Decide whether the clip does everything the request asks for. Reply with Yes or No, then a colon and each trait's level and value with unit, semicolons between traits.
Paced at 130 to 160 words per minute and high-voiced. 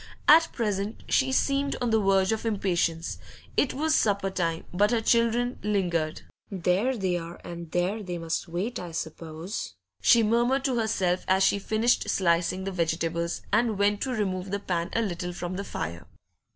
No: average, 175 wpm; high, 195 Hz